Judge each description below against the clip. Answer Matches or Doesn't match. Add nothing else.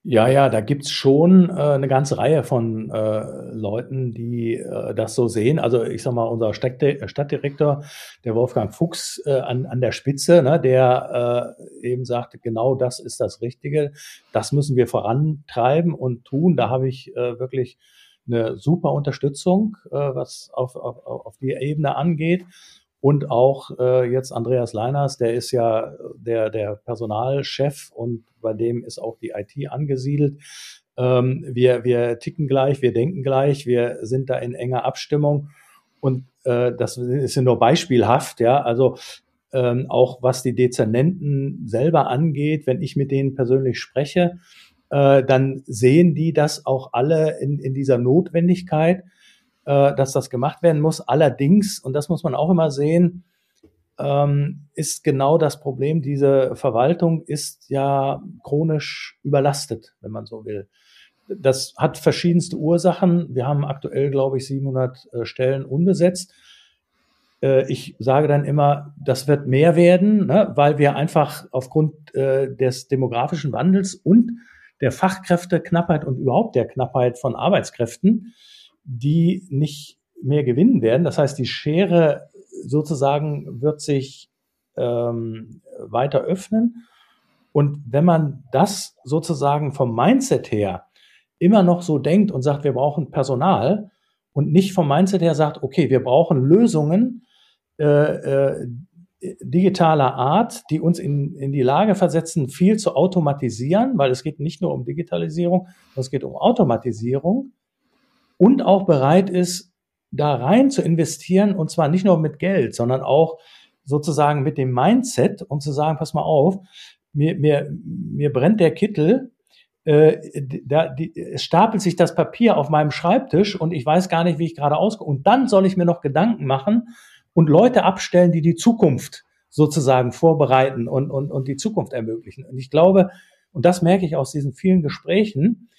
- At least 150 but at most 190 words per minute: Matches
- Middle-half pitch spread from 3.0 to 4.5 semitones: Doesn't match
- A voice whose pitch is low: Doesn't match